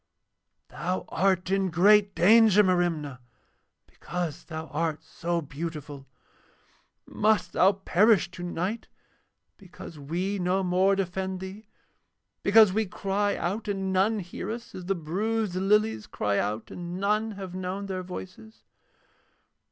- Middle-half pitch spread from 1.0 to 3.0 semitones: Yes, average, 2.7 semitones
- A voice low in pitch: No, medium, 185 Hz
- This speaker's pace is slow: Yes, slow, 125 wpm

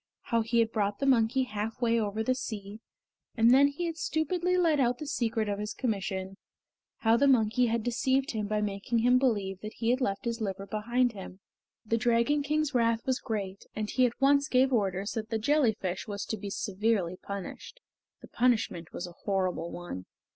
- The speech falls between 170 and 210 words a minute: Yes, average, 195 wpm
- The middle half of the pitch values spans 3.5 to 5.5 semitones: Yes, average, 3.9 semitones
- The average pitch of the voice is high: Yes, high, 225 Hz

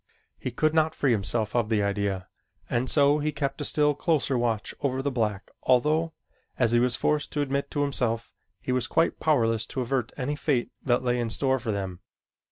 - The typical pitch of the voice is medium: No, low, 125 Hz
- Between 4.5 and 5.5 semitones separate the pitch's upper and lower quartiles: No, average, 4.0 semitones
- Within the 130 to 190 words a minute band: No, average, 200 wpm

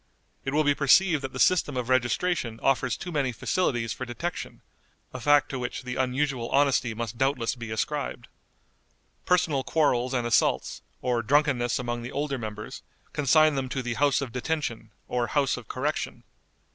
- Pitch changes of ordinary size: Yes, average, 3.3 semitones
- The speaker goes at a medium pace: Yes, average, 170 wpm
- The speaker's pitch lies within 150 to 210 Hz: No, low, 130 Hz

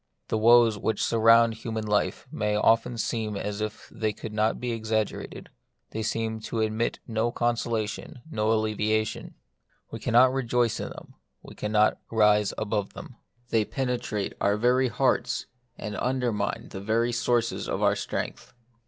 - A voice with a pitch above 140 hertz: No, low, 110 Hz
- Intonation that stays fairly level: Yes, narrow, 1.7 semitones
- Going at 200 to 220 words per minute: No, average, 155 wpm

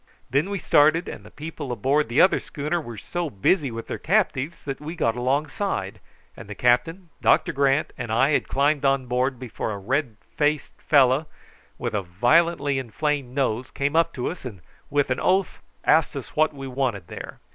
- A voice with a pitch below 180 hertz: Yes, medium, 140 Hz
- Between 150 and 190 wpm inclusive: Yes, average, 185 wpm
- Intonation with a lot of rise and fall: No, average, 3.9 semitones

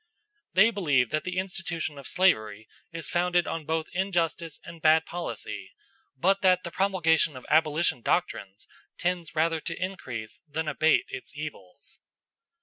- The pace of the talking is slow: No, average, 145 wpm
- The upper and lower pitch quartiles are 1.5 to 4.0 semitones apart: Yes, average, 3.0 semitones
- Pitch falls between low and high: Yes, medium, 165 Hz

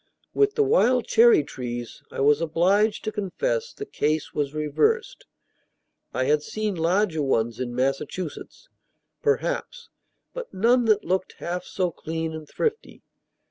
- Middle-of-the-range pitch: Yes, medium, 180 Hz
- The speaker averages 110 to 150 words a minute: Yes, average, 140 wpm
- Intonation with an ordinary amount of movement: No, wide, 8.6 semitones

